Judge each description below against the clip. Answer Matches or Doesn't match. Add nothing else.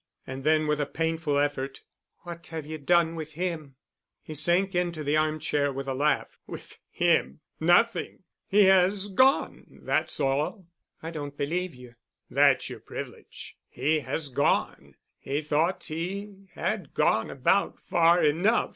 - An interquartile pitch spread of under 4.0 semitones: Matches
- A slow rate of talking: Doesn't match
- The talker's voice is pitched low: Doesn't match